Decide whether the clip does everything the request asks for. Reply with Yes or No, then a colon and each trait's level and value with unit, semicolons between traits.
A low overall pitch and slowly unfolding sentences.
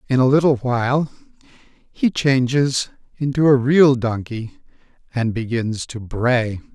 Yes: low, 125 Hz; slow, 125 wpm